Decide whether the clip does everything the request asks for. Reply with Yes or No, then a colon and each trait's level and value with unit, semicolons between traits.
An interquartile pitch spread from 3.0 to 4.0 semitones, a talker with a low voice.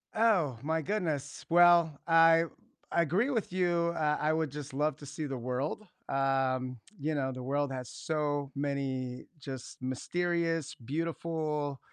No: average, 3.5 semitones; medium, 150 Hz